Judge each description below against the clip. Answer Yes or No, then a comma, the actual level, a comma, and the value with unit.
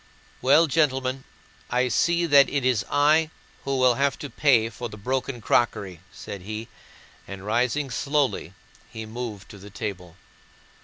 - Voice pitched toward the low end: Yes, low, 125 Hz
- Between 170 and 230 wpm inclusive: No, average, 150 wpm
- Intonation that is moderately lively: Yes, average, 4.6 semitones